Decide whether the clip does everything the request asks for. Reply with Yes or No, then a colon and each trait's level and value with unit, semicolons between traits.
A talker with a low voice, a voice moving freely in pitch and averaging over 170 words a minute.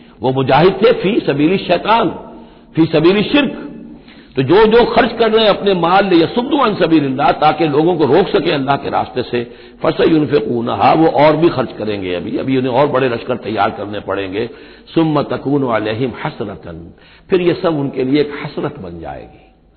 No: medium, 145 Hz; wide, 6.5 semitones; fast, 190 wpm